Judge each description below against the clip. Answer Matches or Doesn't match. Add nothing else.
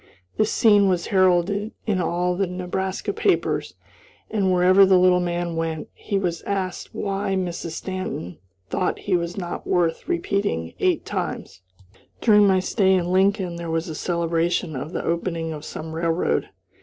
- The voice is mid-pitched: Matches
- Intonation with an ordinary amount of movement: Doesn't match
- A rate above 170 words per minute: Doesn't match